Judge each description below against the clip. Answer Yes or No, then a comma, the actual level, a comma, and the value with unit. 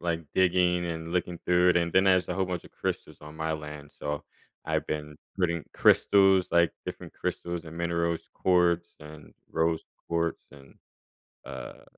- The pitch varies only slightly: Yes, narrow, 2.1 semitones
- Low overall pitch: Yes, very low, 85 Hz